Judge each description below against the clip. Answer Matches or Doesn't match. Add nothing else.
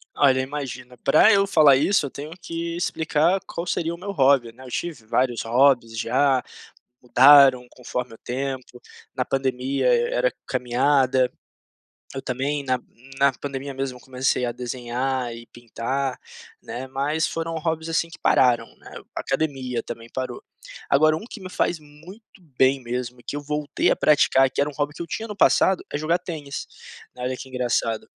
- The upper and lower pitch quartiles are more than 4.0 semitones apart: Doesn't match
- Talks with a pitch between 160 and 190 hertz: Doesn't match